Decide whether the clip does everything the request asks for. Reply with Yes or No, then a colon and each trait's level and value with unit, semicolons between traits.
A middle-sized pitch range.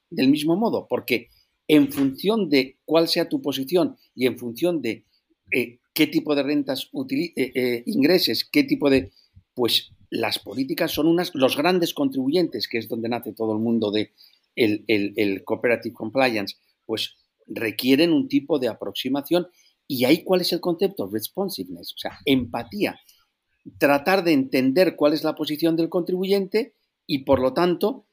No: wide, 7.3 semitones